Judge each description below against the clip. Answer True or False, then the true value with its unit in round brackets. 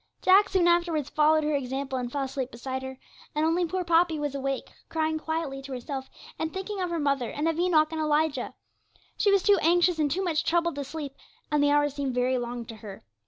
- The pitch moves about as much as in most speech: True (3.7 semitones)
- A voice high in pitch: True (300 Hz)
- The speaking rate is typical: False (220 wpm)